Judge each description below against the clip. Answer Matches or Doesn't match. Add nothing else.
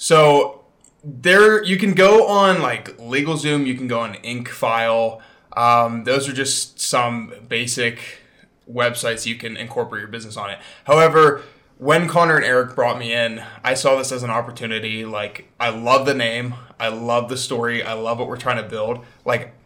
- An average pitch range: Matches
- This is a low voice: Matches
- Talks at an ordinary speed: Matches